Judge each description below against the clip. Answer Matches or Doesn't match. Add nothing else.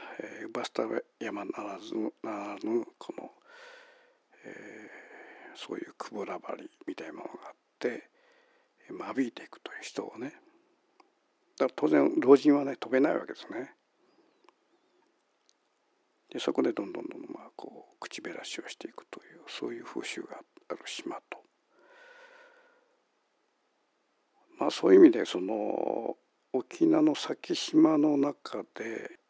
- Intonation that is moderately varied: Doesn't match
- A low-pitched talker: Doesn't match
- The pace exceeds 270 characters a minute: Doesn't match